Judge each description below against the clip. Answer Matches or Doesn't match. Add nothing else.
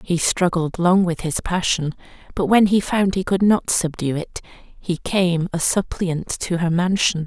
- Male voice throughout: Doesn't match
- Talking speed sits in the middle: Matches